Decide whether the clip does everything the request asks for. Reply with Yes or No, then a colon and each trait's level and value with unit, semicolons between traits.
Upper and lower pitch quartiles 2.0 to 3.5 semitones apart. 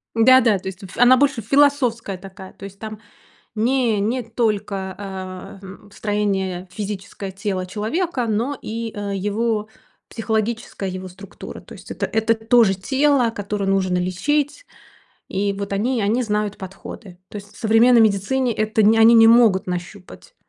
Yes: average, 3.1 semitones